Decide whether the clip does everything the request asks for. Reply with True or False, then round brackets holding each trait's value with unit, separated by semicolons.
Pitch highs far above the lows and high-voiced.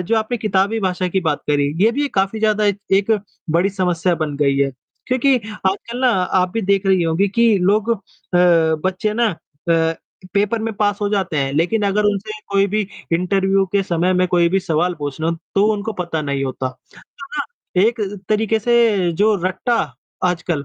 False (3.9 semitones; 195 Hz)